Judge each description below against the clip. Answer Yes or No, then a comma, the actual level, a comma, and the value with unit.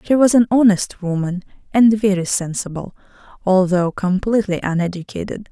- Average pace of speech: No, slow, 120 wpm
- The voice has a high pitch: Yes, high, 195 Hz